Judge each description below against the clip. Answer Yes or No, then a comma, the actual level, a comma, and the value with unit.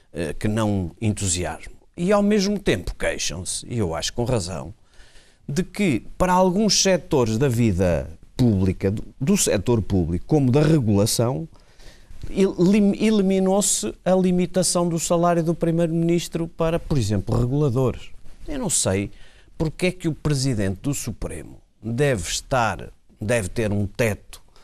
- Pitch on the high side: No, low, 130 Hz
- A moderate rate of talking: Yes, average, 130 wpm